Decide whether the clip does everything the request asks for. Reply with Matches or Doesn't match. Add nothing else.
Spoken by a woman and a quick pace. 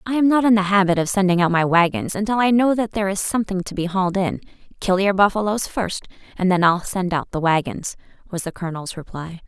Matches